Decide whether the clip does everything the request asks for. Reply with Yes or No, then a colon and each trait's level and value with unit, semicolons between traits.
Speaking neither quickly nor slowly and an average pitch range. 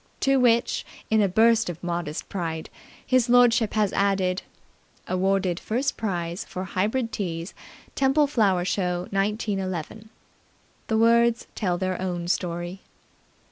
No: slow, 125 wpm; average, 4.3 semitones